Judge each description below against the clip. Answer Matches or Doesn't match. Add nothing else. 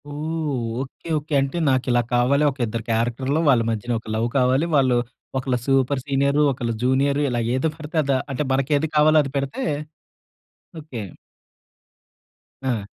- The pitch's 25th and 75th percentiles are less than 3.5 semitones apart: Matches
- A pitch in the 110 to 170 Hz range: Matches